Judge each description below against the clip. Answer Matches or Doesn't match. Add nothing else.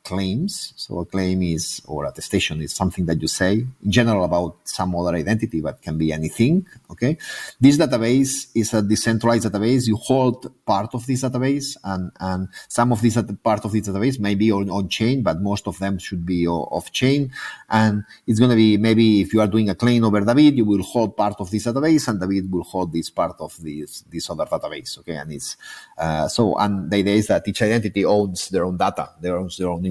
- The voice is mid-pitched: Doesn't match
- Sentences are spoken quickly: Matches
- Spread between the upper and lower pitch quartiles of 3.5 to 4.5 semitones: Matches